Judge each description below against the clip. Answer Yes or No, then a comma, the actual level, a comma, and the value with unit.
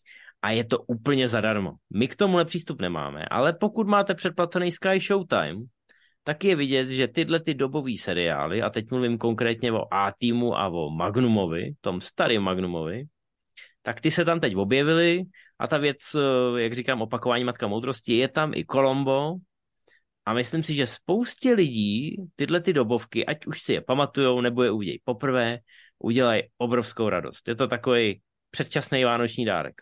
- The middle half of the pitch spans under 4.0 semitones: No, wide, 5.5 semitones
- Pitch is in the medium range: No, low, 125 Hz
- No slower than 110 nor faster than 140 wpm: No, average, 165 wpm